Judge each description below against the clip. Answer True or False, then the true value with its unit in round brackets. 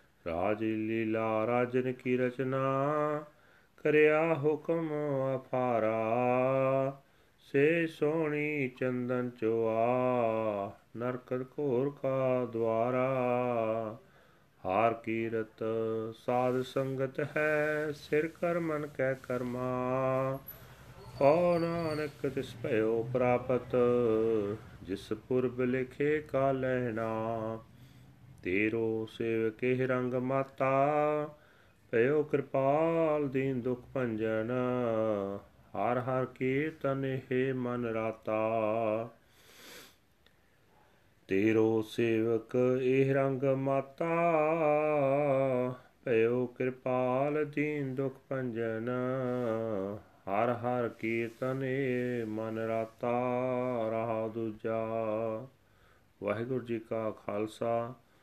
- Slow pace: True (75 wpm)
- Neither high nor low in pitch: False (125 Hz)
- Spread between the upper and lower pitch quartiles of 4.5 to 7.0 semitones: False (3.2 semitones)